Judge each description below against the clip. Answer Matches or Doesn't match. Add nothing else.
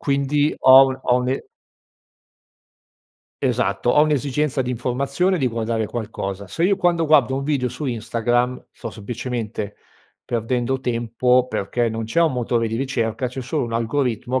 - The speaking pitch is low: Matches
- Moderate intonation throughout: Matches